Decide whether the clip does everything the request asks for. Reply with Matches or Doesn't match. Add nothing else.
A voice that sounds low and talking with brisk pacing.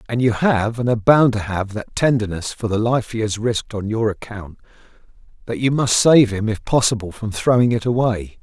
Matches